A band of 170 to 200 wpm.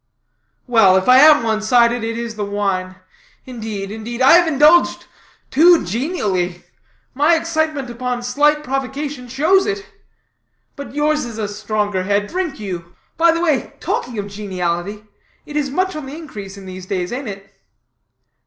No: average, 160 wpm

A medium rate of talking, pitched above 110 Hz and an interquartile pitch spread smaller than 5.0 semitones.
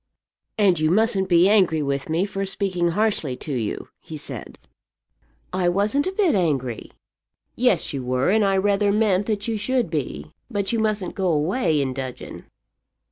No: average, 170 wpm; high, 190 Hz; wide, 5.4 semitones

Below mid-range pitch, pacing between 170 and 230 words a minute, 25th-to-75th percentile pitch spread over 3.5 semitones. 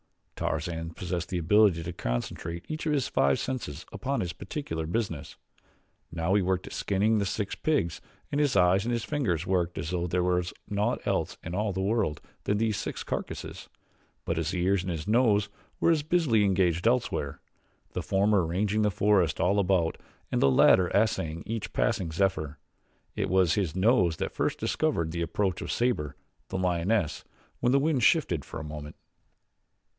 Yes: very low, 95 Hz; average, 180 wpm; average, 4.2 semitones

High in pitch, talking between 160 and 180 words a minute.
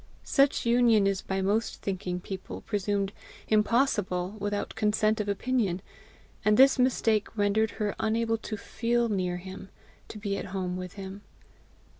No: high, 205 Hz; average, 145 wpm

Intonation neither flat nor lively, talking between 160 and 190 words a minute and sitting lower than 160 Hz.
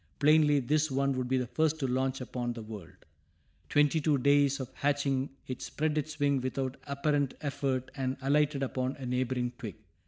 No: narrow, 2.1 semitones; average, 180 wpm; low, 135 Hz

